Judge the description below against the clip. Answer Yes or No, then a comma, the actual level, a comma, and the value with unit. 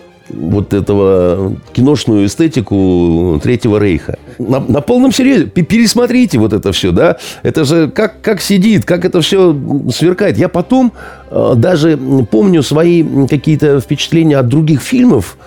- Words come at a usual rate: Yes, average, 135 wpm